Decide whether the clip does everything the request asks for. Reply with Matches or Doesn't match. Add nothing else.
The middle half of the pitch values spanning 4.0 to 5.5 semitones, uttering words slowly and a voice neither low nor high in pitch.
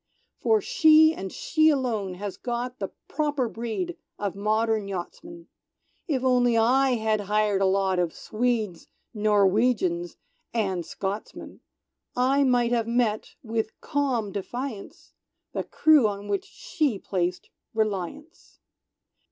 Doesn't match